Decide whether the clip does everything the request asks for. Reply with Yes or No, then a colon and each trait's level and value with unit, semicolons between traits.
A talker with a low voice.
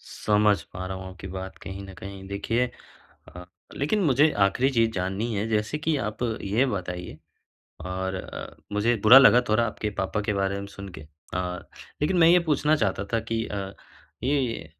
Yes: low, 105 Hz